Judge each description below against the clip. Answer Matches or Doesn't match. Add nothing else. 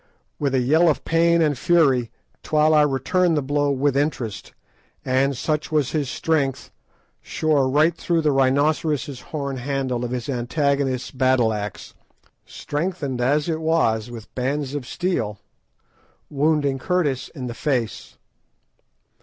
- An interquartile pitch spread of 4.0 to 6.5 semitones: Doesn't match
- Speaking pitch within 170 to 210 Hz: Doesn't match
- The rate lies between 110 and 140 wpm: Matches